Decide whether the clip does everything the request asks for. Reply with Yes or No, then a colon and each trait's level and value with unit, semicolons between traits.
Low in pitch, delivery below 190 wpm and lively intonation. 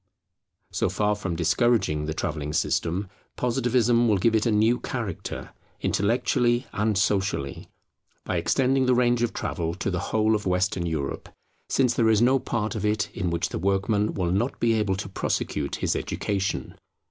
No: low, 105 Hz; average, 170 wpm; average, 4.4 semitones